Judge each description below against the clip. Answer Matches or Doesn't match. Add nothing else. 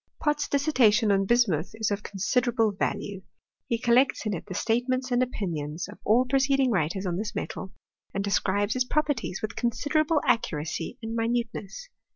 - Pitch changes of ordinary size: Matches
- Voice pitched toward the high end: Matches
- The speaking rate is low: Doesn't match